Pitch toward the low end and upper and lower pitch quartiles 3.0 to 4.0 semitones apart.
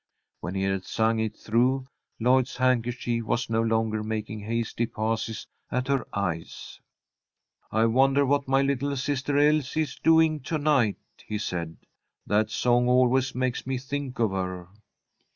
Yes: low, 120 Hz; average, 3.5 semitones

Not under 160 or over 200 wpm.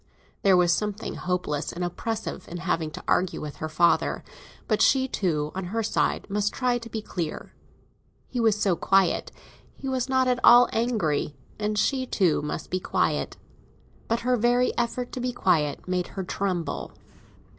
Yes: average, 170 wpm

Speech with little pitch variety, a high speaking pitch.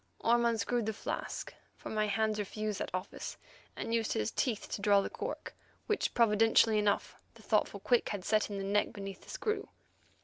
Yes: narrow, 2.1 semitones; high, 215 Hz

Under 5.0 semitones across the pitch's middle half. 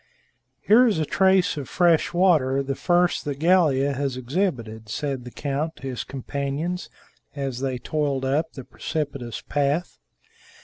Yes: average, 4.3 semitones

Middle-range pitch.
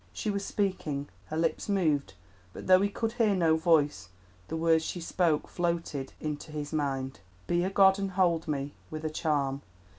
Yes: medium, 160 Hz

